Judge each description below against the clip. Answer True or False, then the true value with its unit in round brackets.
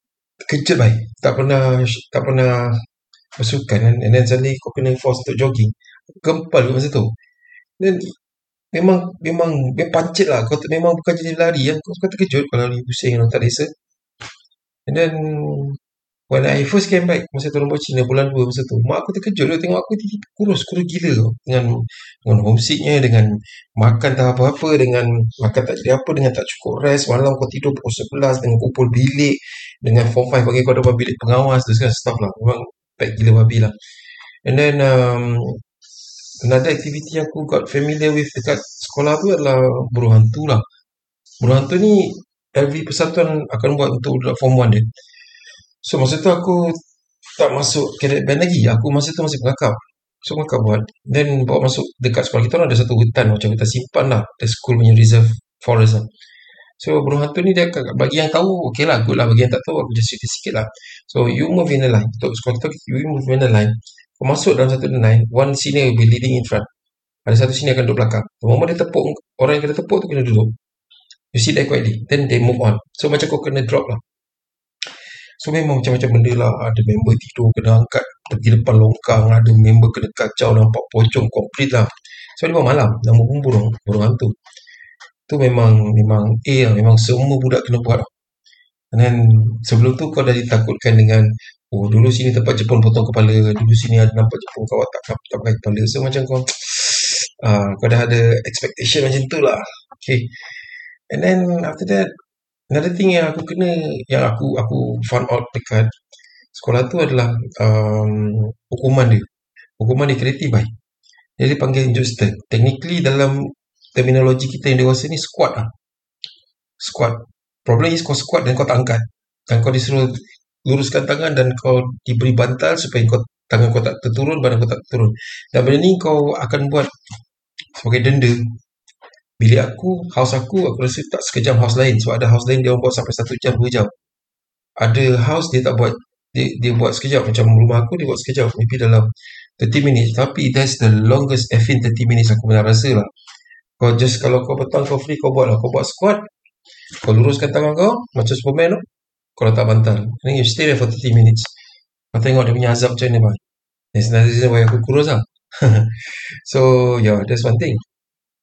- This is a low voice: True (125 Hz)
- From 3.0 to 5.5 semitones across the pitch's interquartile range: True (4.0 semitones)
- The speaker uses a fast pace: True (190 wpm)